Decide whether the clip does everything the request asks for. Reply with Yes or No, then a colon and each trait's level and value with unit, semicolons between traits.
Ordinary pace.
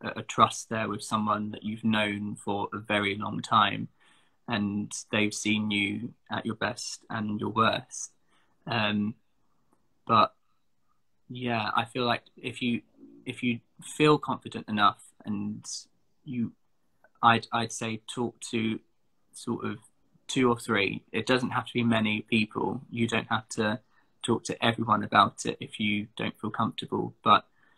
Yes: average, 150 wpm